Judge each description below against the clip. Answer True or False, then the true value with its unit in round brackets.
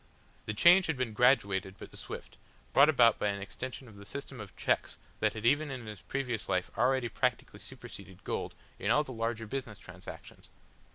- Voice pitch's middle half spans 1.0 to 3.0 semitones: False (4.7 semitones)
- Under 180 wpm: False (185 wpm)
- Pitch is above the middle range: False (115 Hz)